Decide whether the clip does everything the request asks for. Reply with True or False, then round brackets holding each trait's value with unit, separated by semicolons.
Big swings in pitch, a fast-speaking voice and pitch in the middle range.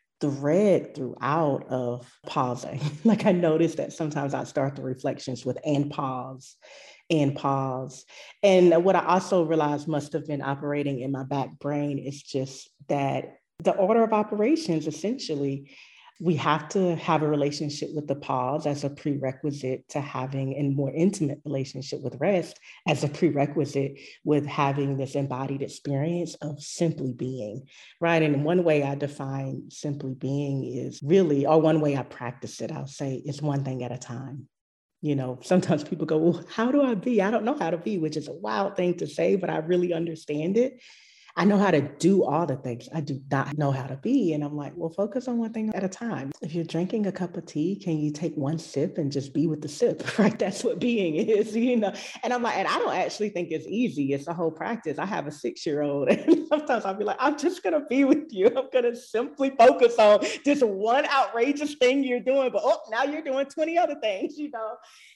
True (6.9 semitones; 210 wpm; 155 Hz)